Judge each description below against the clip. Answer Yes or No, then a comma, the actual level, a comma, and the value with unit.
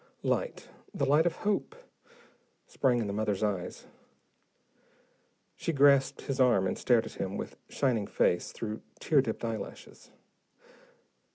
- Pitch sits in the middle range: No, low, 120 Hz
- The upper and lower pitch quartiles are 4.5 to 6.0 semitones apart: Yes, average, 4.8 semitones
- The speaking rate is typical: No, slow, 130 wpm